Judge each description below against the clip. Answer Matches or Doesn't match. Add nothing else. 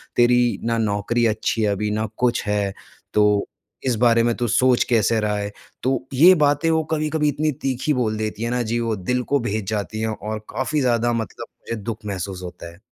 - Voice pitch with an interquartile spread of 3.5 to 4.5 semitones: Doesn't match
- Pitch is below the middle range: Matches